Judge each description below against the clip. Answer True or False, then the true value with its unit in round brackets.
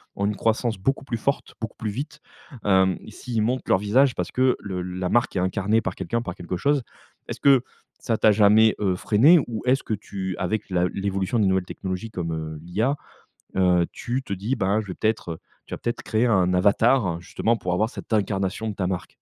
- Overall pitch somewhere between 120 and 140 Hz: False (105 Hz)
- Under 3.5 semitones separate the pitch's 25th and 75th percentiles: False (3.9 semitones)